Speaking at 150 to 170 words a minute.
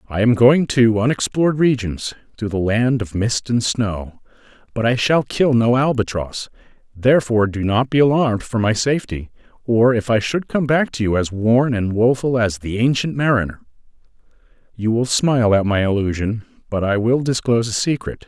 No: average, 180 wpm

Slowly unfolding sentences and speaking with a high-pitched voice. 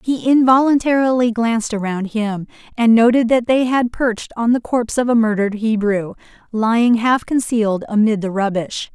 No: average, 160 wpm; high, 230 Hz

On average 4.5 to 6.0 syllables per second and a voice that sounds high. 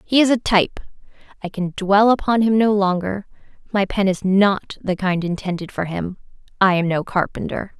Yes: 5.0 syllables/s; high, 195 Hz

